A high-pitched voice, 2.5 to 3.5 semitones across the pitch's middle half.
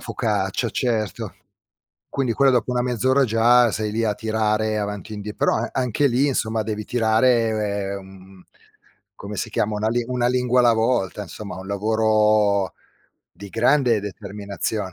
No: low, 110 Hz; average, 2.8 semitones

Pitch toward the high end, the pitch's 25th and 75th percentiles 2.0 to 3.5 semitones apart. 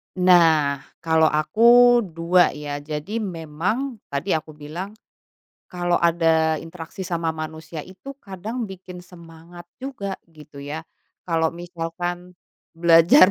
No: medium, 170 Hz; narrow, 2.6 semitones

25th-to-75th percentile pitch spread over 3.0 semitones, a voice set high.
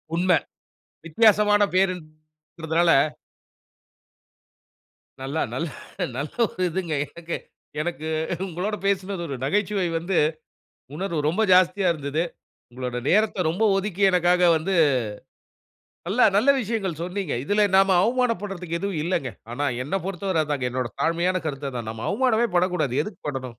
No: average, 4.0 semitones; medium, 180 Hz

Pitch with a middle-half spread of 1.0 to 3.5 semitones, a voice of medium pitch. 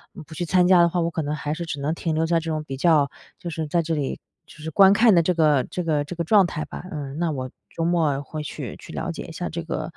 Yes: narrow, 2.4 semitones; medium, 160 Hz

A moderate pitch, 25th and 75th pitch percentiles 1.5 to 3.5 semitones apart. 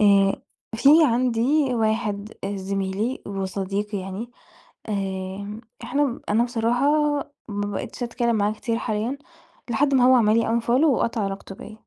No: high, 220 Hz; average, 3.2 semitones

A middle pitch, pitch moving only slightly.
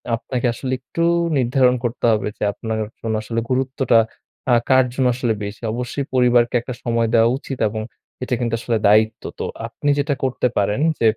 No: low, 120 Hz; narrow, 2.3 semitones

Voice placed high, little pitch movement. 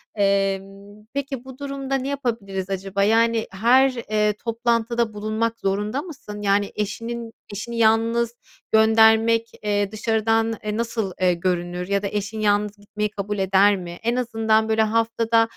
Yes: high, 220 Hz; narrow, 2.3 semitones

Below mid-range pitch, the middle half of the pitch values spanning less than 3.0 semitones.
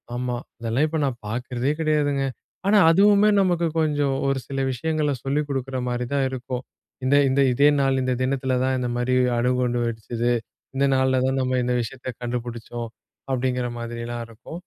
Yes: low, 130 Hz; narrow, 2.5 semitones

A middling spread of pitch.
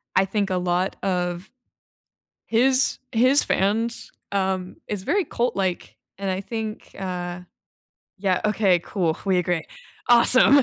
Yes: average, 3.8 semitones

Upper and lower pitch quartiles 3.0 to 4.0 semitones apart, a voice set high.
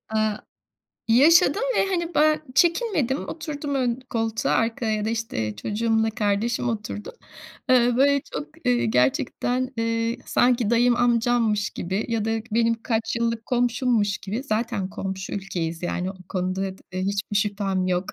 Yes: average, 3.6 semitones; high, 225 Hz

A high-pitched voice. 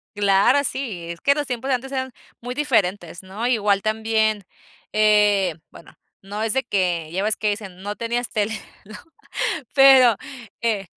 Yes: high, 215 Hz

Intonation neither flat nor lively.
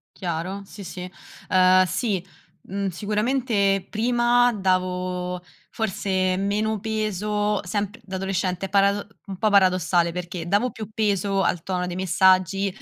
No: narrow, 2.3 semitones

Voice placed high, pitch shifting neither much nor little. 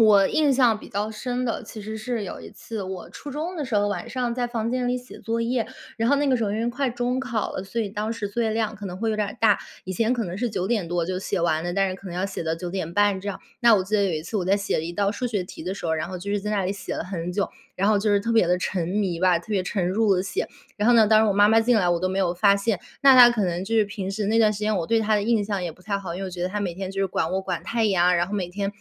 Yes: high, 205 Hz; average, 3.4 semitones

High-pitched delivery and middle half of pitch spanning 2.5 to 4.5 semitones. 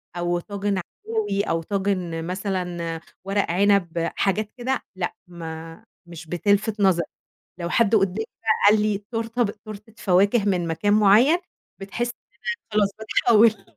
Yes: high, 200 Hz; average, 3.5 semitones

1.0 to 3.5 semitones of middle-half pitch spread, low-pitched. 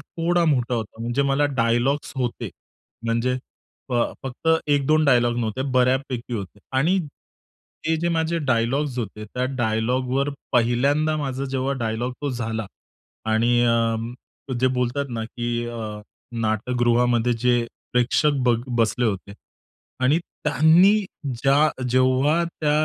Yes: average, 3.1 semitones; low, 125 Hz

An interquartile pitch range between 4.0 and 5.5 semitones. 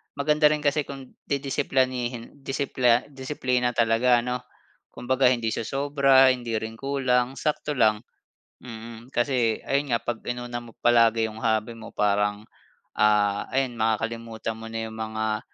No: average, 3.0 semitones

